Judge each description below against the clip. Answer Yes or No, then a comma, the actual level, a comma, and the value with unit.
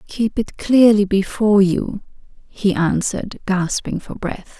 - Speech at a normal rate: No, slow, 130 wpm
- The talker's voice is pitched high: Yes, high, 200 Hz